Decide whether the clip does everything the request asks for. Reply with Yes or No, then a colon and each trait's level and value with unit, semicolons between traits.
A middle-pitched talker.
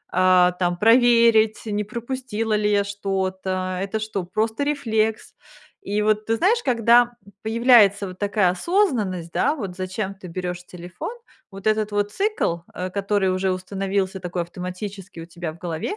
No: high, 200 Hz